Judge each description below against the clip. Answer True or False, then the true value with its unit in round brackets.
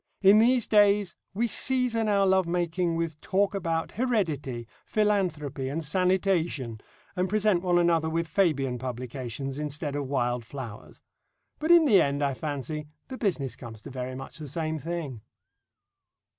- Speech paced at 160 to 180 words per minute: False (150 wpm)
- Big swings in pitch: True (6.2 semitones)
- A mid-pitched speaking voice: True (165 Hz)